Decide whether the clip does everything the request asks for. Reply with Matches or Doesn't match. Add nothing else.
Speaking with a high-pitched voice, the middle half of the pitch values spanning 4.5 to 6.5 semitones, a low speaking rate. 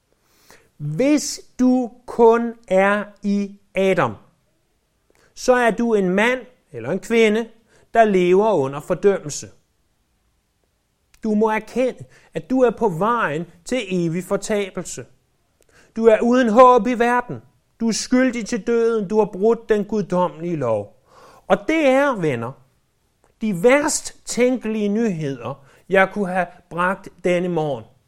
Matches